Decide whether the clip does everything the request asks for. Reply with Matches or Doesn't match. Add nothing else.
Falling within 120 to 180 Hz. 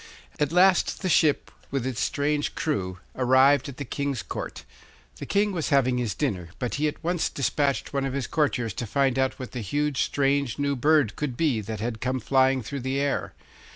Matches